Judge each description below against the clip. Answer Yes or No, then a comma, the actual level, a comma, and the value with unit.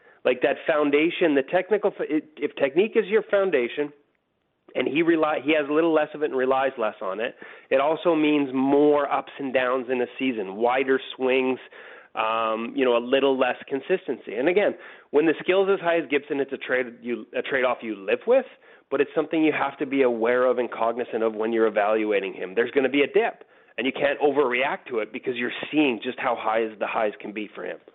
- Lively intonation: No, average, 4.7 semitones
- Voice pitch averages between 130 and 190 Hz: Yes, medium, 140 Hz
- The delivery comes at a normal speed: No, fast, 225 wpm